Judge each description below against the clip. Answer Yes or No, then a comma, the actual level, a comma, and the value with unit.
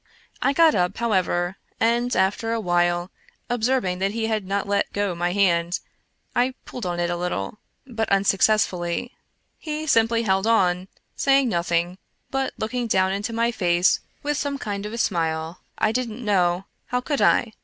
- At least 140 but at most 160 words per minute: No, average, 175 wpm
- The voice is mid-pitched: No, high, 205 Hz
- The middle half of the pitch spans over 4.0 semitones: Yes, average, 4.8 semitones